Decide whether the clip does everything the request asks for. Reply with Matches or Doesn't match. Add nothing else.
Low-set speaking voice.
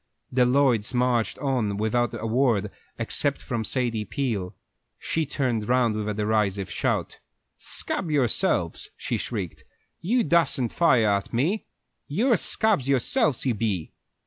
Matches